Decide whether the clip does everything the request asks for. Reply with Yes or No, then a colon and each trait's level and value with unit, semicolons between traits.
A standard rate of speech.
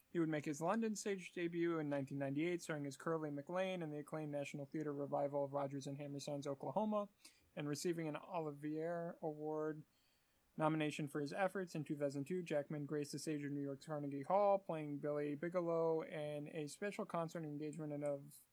Yes: average, 170 wpm